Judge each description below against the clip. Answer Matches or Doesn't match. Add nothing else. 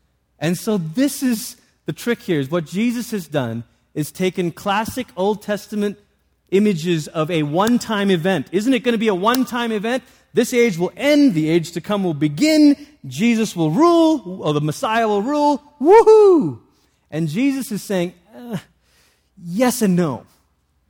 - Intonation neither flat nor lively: Doesn't match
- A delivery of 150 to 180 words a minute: Matches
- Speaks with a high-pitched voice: Matches